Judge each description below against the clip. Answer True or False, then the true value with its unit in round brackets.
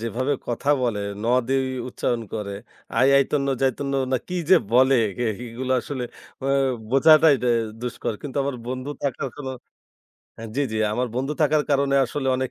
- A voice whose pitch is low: True (130 Hz)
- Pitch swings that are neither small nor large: False (2.3 semitones)